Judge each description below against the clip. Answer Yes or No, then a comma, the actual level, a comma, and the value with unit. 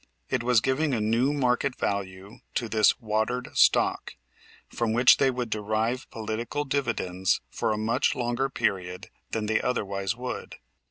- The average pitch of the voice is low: Yes, low, 115 Hz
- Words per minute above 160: No, average, 150 wpm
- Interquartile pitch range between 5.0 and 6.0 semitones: No, average, 2.8 semitones